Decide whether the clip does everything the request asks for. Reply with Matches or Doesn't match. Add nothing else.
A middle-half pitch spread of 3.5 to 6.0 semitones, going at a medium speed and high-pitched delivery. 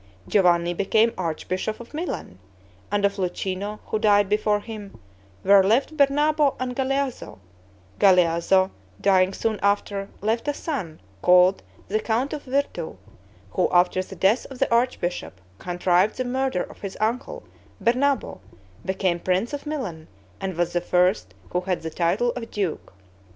Matches